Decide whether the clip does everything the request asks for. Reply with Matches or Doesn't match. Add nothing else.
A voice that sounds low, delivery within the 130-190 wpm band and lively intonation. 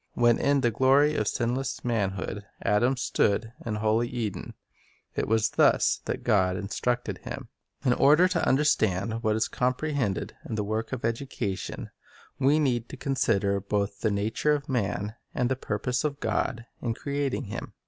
Doesn't match